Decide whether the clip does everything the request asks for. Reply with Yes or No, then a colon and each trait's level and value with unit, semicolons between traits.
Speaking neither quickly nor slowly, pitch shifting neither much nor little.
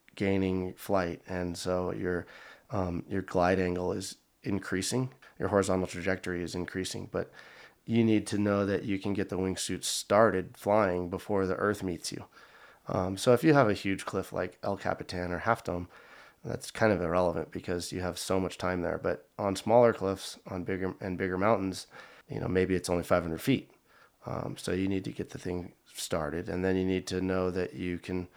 No: average, 195 wpm; narrow, 1.8 semitones